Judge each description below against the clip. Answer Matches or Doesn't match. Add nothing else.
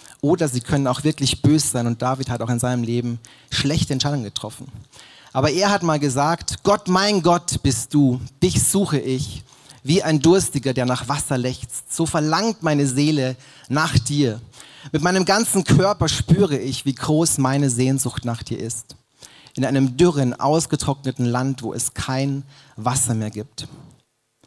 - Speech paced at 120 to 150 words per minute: Doesn't match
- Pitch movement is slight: Doesn't match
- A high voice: Doesn't match